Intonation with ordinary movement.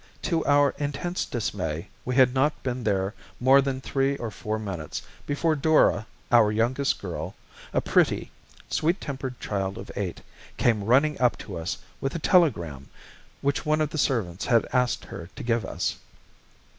No: wide, 5.8 semitones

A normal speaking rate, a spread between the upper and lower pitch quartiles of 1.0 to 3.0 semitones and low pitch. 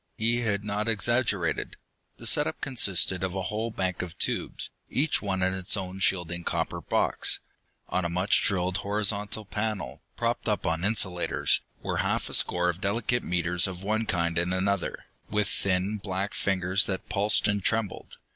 Yes: average, 170 wpm; narrow, 2.6 semitones; very low, 95 Hz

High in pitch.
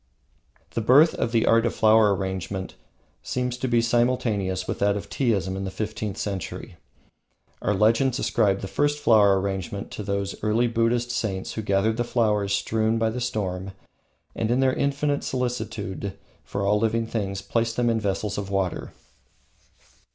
No: low, 110 Hz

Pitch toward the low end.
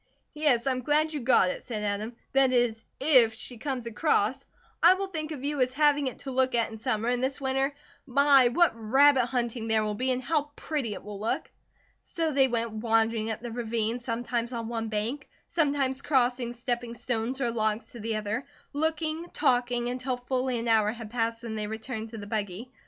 No: high, 245 Hz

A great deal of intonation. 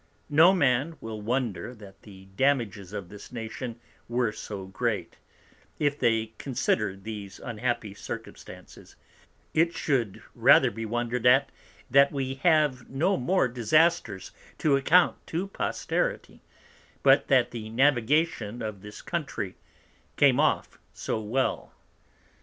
No: average, 4.8 semitones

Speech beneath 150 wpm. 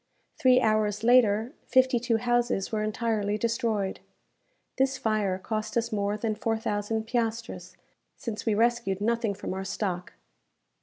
Yes: average, 140 wpm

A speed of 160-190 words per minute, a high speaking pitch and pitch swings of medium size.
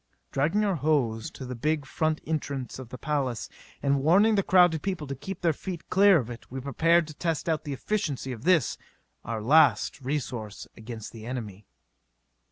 No: average, 180 wpm; medium, 145 Hz; average, 4.8 semitones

